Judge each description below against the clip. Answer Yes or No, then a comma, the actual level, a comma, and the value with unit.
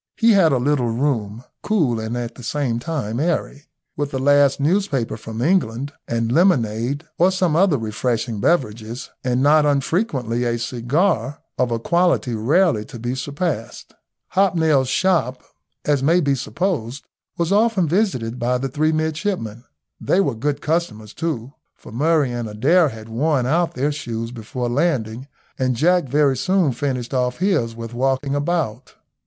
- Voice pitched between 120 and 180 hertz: Yes, low, 135 Hz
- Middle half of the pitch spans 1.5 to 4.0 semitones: No, wide, 5.5 semitones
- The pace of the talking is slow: No, average, 155 wpm